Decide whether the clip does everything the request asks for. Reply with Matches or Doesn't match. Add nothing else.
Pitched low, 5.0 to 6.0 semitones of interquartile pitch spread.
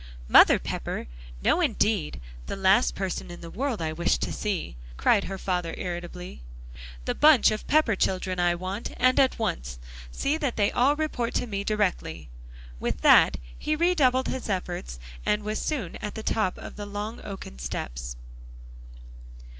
Doesn't match